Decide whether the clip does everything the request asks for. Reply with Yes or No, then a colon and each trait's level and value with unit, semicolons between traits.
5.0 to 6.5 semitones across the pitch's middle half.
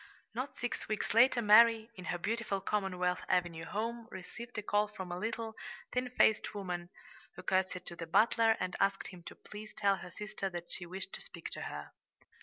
No: average, 3.8 semitones